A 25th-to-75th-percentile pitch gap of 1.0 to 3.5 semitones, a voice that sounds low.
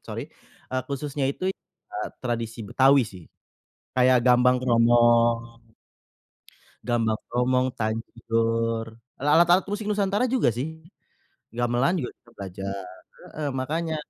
No: average, 4.2 semitones; low, 125 Hz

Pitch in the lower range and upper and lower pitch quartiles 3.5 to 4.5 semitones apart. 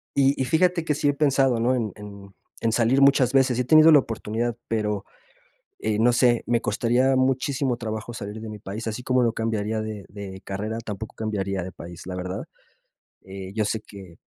Yes: low, 115 Hz; average, 3.8 semitones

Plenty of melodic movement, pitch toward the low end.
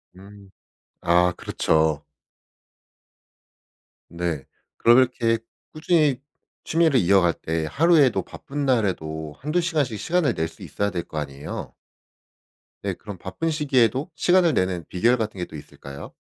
Yes: wide, 8.8 semitones; low, 105 Hz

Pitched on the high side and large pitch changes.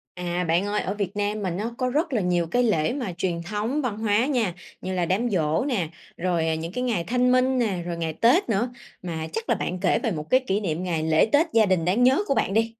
Yes: high, 205 Hz; wide, 5.7 semitones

